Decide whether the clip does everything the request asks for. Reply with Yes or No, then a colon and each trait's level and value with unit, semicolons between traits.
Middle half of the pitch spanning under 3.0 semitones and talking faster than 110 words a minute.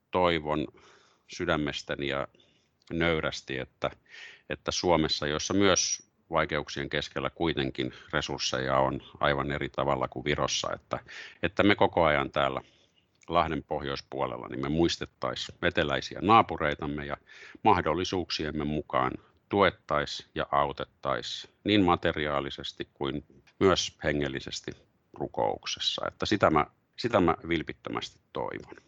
No: narrow, 2.6 semitones; average, 105 wpm